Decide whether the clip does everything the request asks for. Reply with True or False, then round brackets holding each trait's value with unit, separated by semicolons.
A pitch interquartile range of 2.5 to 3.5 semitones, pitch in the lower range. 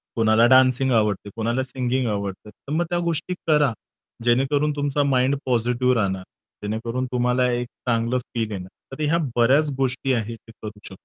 True (2.9 semitones; 125 Hz)